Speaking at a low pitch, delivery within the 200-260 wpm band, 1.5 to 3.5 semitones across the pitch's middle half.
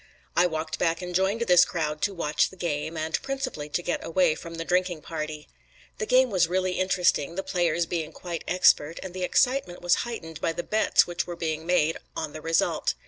No: medium, 175 Hz; fast, 205 wpm; narrow, 2.4 semitones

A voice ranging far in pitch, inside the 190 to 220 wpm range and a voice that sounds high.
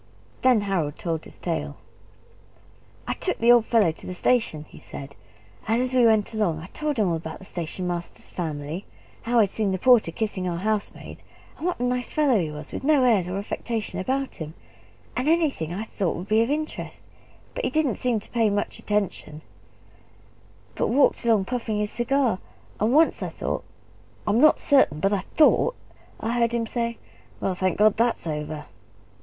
Yes: wide, 5.8 semitones; average, 195 wpm; high, 215 Hz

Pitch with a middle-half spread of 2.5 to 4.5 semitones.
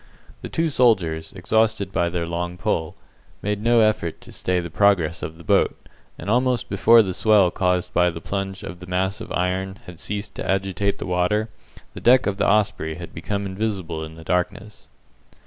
Yes: average, 3.3 semitones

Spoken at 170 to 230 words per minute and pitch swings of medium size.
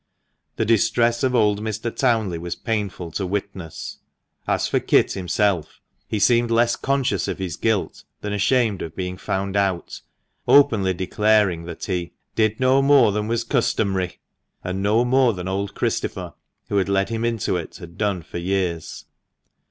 No: average, 160 wpm; average, 3.7 semitones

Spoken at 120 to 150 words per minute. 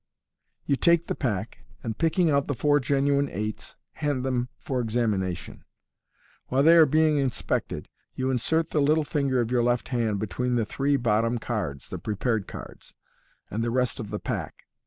No: average, 175 wpm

